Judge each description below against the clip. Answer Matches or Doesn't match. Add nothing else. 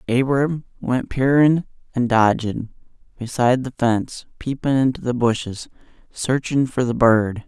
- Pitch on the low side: Matches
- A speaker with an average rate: Doesn't match